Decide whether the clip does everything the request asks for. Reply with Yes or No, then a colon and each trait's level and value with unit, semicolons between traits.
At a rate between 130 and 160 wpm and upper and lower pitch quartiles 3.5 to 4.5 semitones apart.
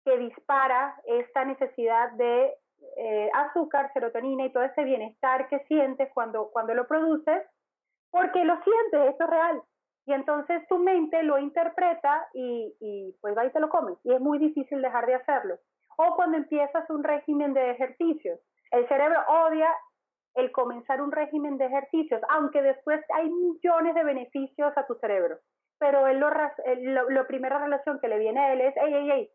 No: average, 175 wpm; average, 3.8 semitones